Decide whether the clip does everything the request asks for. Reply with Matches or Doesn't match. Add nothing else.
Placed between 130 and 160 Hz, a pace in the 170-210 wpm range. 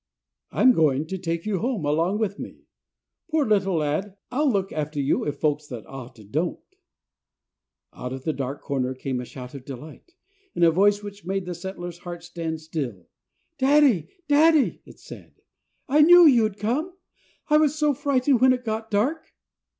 Doesn't match